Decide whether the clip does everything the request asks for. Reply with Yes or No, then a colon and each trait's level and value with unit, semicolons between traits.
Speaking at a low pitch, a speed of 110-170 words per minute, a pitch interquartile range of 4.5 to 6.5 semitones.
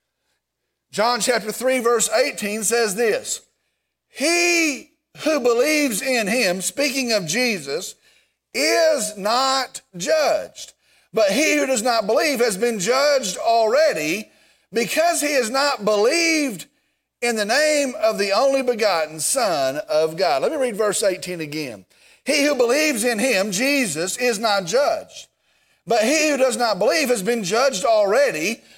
No: very high, 250 Hz; average, 140 wpm; average, 5.2 semitones